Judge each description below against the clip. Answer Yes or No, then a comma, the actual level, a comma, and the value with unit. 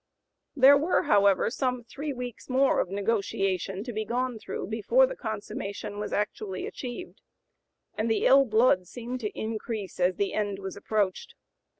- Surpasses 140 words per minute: Yes, average, 160 wpm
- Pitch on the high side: Yes, high, 220 Hz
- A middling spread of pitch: Yes, average, 3.9 semitones